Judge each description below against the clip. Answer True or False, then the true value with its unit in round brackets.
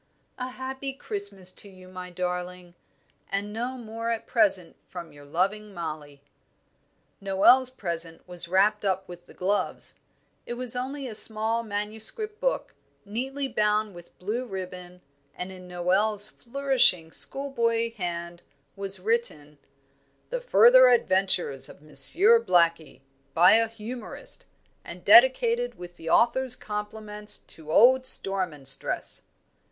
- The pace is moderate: False (130 wpm)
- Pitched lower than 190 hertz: False (205 Hz)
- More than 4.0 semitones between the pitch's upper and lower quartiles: True (5.1 semitones)